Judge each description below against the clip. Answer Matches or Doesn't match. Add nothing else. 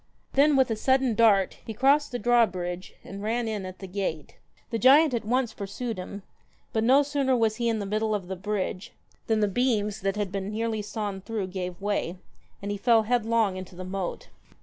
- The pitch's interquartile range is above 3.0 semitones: Matches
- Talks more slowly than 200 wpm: Doesn't match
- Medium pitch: Doesn't match